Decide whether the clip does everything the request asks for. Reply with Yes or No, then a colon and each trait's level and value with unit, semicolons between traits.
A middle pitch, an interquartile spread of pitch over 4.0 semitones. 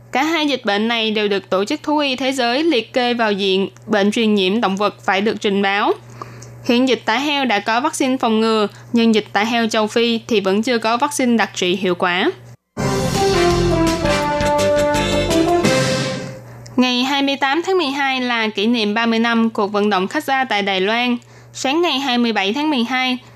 No: high, 230 Hz; average, 4.7 semitones